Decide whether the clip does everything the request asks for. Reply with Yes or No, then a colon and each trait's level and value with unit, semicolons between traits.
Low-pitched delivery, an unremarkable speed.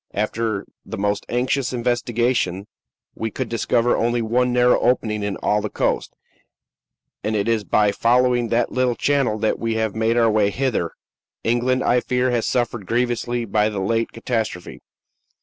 Yes: low, 115 Hz; average, 160 wpm